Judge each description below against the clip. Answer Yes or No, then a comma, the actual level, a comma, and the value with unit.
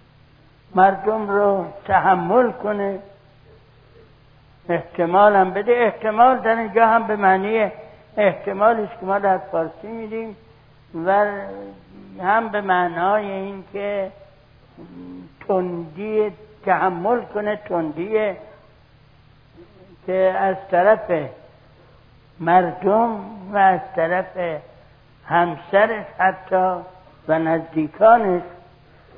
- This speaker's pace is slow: Yes, slow, 80 wpm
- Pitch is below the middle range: No, medium, 185 Hz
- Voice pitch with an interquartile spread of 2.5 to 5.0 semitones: No, wide, 5.5 semitones